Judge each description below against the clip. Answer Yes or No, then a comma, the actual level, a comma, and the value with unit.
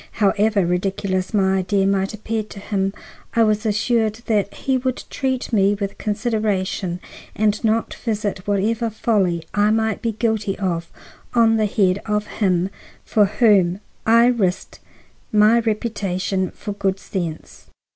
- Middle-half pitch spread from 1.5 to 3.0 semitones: Yes, narrow, 2.4 semitones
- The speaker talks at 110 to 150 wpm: Yes, average, 140 wpm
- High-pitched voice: Yes, high, 205 Hz